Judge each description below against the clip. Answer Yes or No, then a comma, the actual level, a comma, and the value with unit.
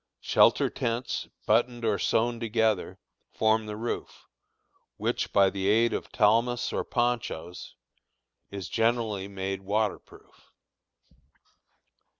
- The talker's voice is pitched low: Yes, low, 110 Hz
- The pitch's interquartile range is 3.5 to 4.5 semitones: No, average, 2.8 semitones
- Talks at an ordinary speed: No, slow, 110 wpm